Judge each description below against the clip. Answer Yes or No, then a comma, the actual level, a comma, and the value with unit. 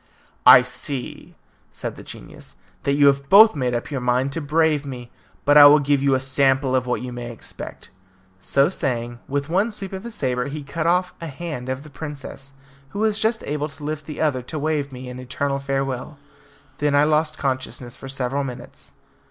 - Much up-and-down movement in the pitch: No, average, 2.9 semitones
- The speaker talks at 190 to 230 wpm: Yes, average, 200 wpm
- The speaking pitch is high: No, medium, 140 Hz